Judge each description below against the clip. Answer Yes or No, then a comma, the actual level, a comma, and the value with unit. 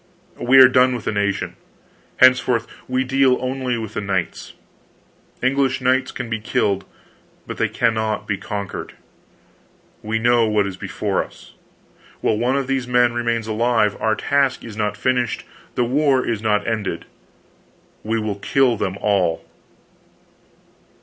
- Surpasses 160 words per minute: No, average, 145 wpm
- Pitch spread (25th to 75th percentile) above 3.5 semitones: No, average, 3.2 semitones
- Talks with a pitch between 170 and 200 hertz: No, low, 115 Hz